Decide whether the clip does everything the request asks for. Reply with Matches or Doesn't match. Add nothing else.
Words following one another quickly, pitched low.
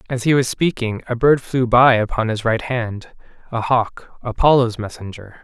Doesn't match